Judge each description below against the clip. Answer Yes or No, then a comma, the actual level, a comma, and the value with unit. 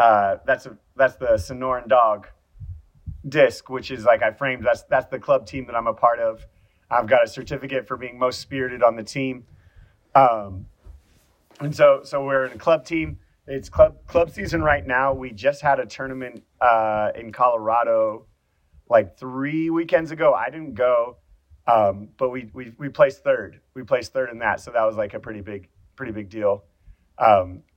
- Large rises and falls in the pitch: Yes, wide, 5.9 semitones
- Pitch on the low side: Yes, low, 125 Hz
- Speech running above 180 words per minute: Yes, average, 200 wpm